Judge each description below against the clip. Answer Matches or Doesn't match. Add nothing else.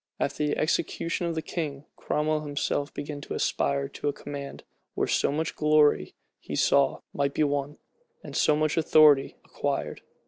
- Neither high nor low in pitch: Matches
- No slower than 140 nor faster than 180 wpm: Matches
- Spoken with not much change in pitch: Matches